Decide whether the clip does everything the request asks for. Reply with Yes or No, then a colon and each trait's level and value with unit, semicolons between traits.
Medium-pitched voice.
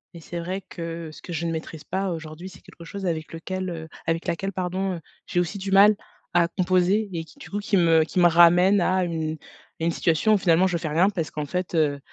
Yes: medium, 175 Hz